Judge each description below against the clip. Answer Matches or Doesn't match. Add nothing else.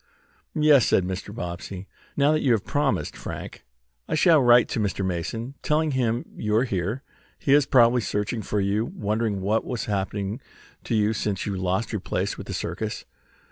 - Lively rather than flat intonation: Doesn't match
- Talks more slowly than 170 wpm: Doesn't match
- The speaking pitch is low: Matches